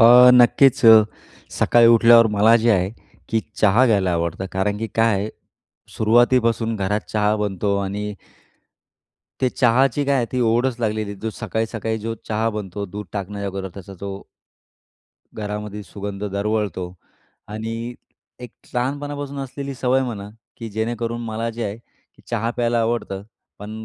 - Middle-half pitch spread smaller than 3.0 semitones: Yes, narrow, 2.6 semitones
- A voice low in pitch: Yes, low, 110 Hz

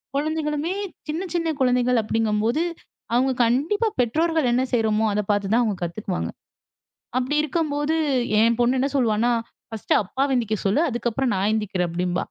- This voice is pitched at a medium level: No, high, 245 Hz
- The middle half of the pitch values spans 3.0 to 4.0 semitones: No, wide, 5.4 semitones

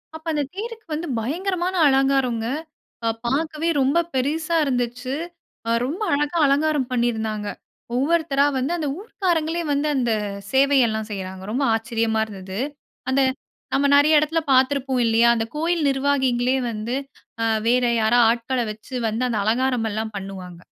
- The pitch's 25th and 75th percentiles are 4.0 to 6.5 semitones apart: Yes, average, 4.9 semitones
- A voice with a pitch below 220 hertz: No, very high, 265 Hz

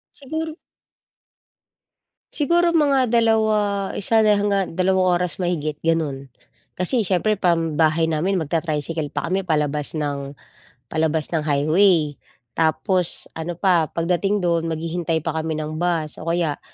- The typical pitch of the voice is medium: Yes, medium, 170 Hz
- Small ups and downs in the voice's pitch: No, average, 4.0 semitones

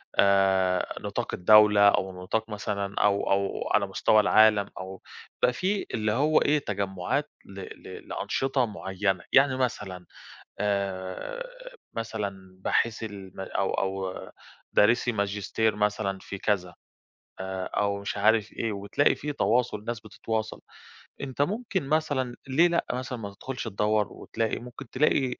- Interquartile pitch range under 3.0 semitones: No, average, 4.0 semitones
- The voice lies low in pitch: Yes, low, 105 Hz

